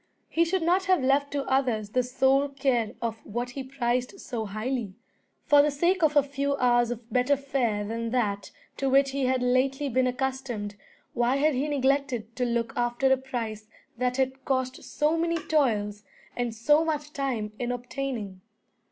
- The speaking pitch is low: No, very high, 260 Hz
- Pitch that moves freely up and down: No, average, 2.8 semitones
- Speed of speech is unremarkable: Yes, average, 180 wpm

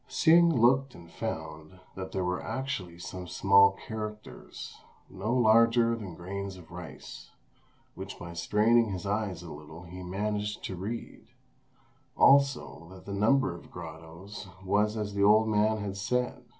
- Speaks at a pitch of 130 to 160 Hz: No, low, 100 Hz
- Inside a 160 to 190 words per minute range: No, average, 150 wpm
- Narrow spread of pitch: No, average, 3.7 semitones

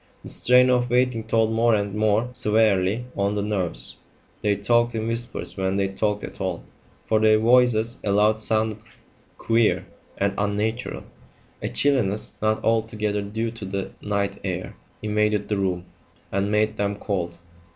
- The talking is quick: No, average, 150 wpm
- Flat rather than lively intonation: Yes, narrow, 2.1 semitones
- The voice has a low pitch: Yes, low, 105 Hz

